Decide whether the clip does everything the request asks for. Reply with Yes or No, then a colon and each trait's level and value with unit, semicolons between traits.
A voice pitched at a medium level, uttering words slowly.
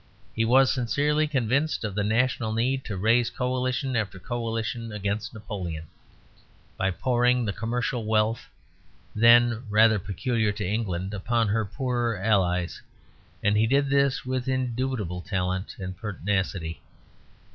No: low, 115 Hz; slow, 130 wpm